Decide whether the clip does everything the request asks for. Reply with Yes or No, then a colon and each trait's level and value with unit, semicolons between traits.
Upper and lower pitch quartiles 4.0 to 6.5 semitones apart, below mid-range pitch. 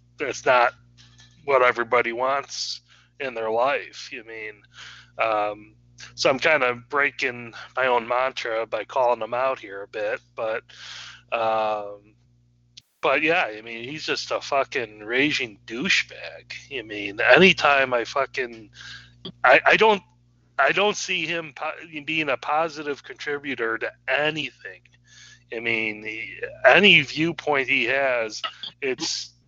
Yes: average, 4.6 semitones; low, 120 Hz